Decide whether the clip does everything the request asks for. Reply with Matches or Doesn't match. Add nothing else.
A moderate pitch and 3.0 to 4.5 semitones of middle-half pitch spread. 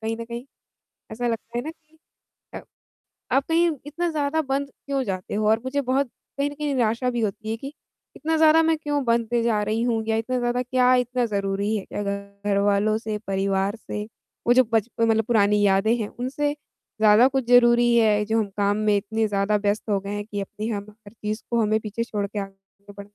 Doesn't match